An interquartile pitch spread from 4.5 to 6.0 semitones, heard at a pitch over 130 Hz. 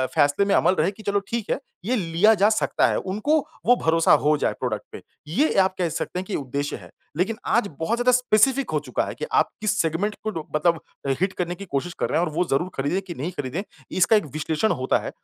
Yes: average, 4.9 semitones; medium, 185 Hz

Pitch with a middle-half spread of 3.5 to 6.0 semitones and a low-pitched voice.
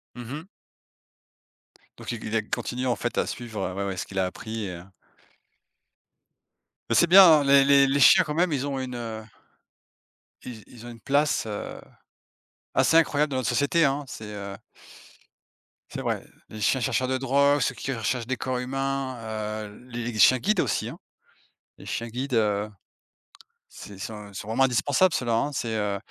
Yes: average, 4.0 semitones; low, 125 Hz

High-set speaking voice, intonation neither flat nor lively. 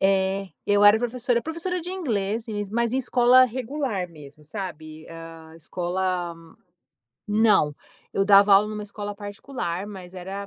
Yes: high, 200 Hz; average, 4.8 semitones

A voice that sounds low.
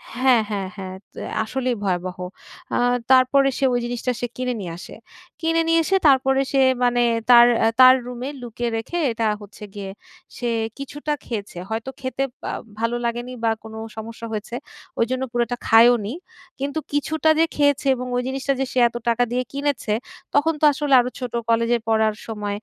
No: high, 245 Hz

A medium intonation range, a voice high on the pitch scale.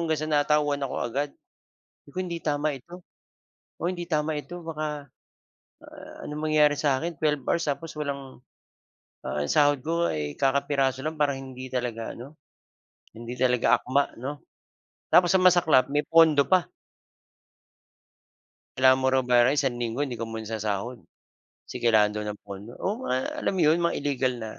No: average, 3.8 semitones; medium, 140 Hz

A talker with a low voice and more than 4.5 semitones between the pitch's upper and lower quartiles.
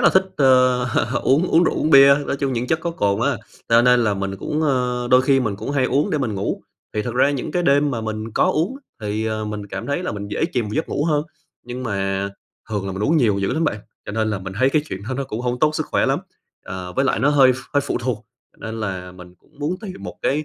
Yes: low, 125 Hz; average, 5.1 semitones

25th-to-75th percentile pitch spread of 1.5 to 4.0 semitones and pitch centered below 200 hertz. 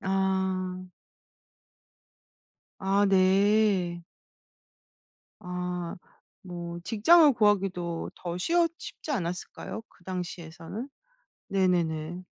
Yes: narrow, 2.5 semitones; medium, 185 Hz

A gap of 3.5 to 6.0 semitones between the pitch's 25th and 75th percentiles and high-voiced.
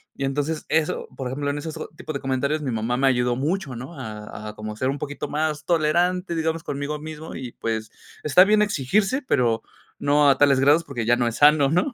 No: average, 3.8 semitones; medium, 145 Hz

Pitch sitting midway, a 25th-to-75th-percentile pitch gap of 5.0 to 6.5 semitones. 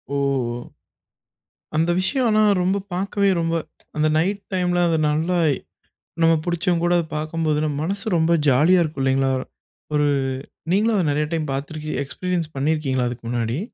No: medium, 160 Hz; average, 3.4 semitones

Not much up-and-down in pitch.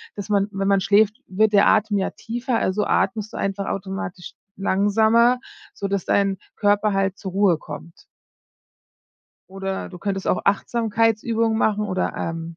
Yes: narrow, 2.0 semitones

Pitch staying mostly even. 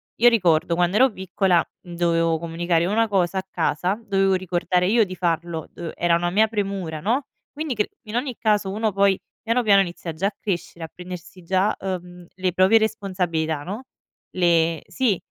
No: average, 3.2 semitones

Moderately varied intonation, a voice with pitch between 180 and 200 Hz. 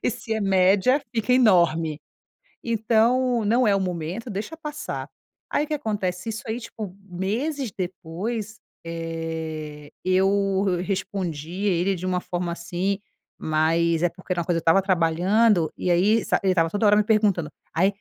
Yes: average, 4.4 semitones; high, 190 Hz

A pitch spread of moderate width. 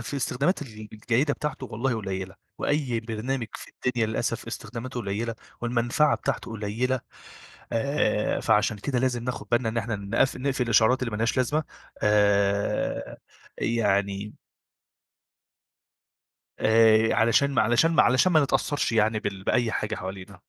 Yes: average, 3.3 semitones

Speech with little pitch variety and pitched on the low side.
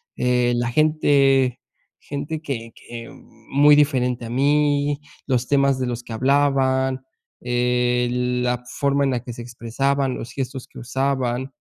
Yes: narrow, 2.2 semitones; low, 130 Hz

